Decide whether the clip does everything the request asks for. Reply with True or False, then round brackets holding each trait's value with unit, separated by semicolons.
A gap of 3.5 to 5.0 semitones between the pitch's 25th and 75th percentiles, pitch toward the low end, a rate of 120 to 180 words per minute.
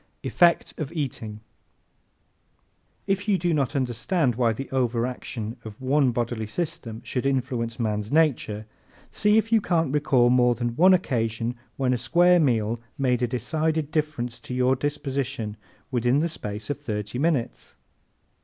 True (4.7 semitones; 130 Hz; 155 wpm)